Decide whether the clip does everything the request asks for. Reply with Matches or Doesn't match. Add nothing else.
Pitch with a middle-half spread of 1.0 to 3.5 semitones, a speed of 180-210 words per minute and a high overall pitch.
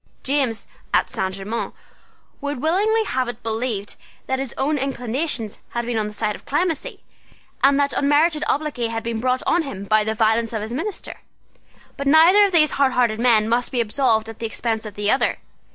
Doesn't match